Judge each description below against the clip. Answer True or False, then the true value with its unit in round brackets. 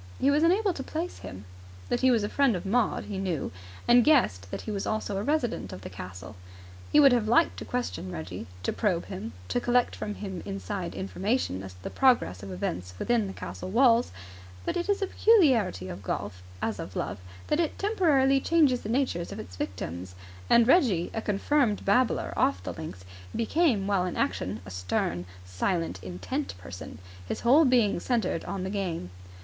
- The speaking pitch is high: True (200 Hz)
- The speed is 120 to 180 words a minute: False (195 wpm)